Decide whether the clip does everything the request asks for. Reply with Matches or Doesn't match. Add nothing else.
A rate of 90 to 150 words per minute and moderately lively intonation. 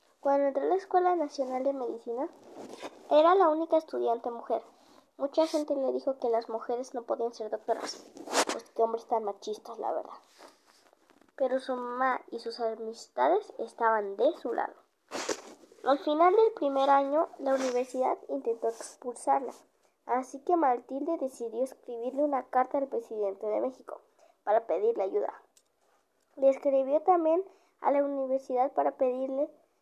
Matches